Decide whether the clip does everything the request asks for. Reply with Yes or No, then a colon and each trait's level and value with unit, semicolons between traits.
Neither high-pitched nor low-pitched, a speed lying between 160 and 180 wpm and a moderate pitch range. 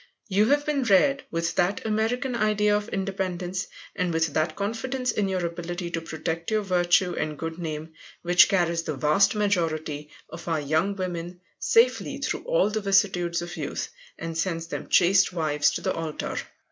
Yes: medium, 180 Hz; average, 170 wpm; average, 3.9 semitones